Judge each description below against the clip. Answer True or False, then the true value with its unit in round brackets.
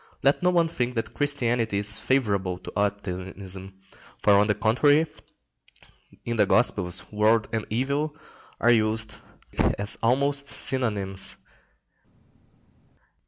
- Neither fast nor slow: False (115 wpm)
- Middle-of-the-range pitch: False (110 Hz)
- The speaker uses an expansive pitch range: False (4.5 semitones)